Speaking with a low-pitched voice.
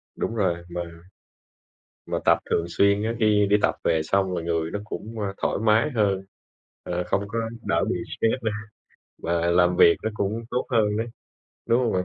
Yes: low, 100 Hz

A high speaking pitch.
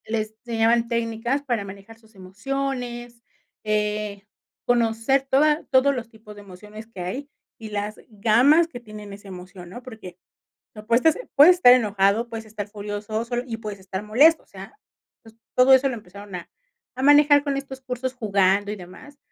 Yes: high, 225 Hz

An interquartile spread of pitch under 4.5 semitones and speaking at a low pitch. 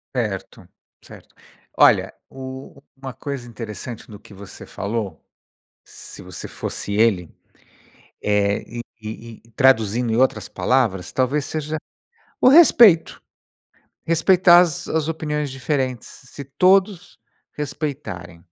No: wide, 5.6 semitones; low, 130 Hz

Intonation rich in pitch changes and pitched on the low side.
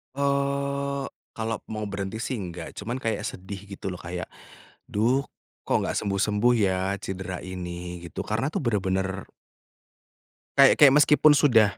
Yes: wide, 6.1 semitones; low, 105 Hz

